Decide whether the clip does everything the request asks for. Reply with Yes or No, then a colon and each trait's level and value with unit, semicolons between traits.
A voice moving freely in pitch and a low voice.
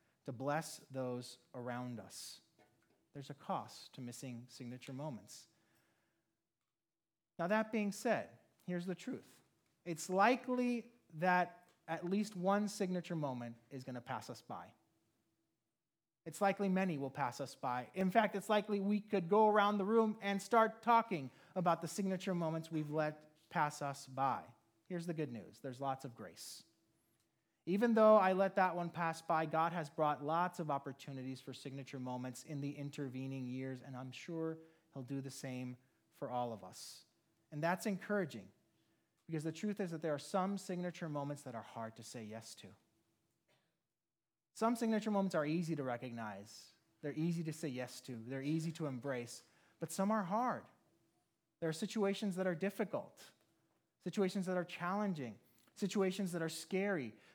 No: wide, 6.4 semitones; medium, 160 Hz